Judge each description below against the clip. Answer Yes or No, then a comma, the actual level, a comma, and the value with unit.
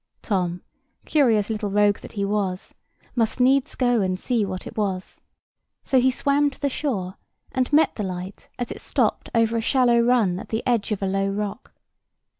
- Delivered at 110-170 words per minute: No, average, 190 wpm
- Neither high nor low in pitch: No, high, 220 Hz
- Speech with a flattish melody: No, average, 4.2 semitones